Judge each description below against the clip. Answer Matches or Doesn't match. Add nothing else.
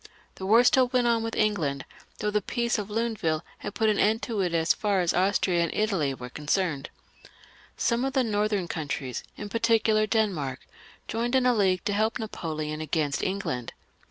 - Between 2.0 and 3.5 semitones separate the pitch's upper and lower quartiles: Doesn't match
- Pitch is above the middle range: Matches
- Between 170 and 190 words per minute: Matches